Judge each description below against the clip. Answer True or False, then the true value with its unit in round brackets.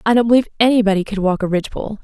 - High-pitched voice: True (210 Hz)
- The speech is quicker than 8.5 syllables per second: True (8.9 syllables/s)